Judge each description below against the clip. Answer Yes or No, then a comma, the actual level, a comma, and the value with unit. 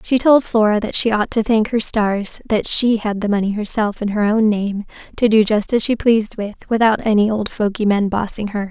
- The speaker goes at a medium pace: No, fast, 235 wpm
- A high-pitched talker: Yes, high, 215 Hz